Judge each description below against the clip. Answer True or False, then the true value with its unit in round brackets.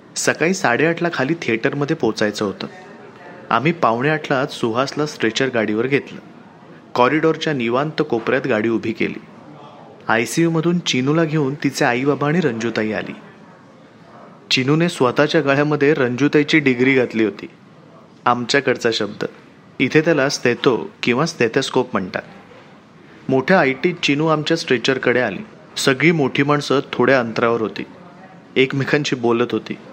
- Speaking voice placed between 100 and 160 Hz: True (135 Hz)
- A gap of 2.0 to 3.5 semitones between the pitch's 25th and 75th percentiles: False (4.5 semitones)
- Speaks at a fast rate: False (120 wpm)